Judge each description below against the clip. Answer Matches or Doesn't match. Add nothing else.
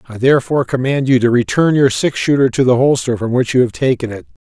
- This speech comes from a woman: Doesn't match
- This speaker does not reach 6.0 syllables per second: Doesn't match